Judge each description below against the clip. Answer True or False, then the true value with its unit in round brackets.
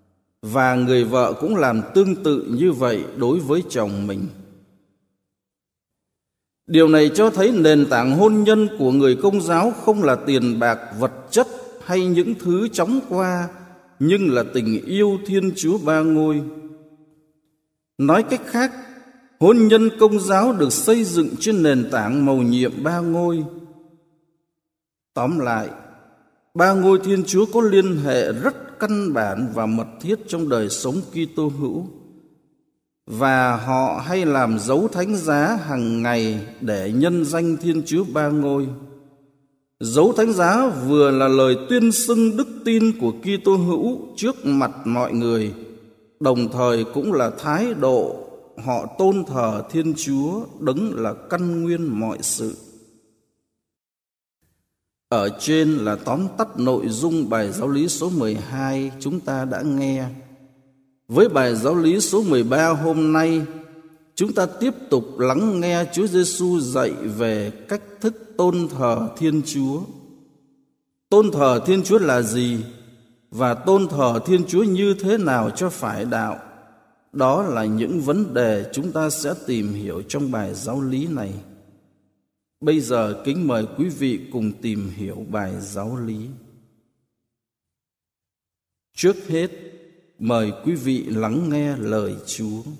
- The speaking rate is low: True (145 wpm)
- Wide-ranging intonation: True (7.7 semitones)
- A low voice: False (150 Hz)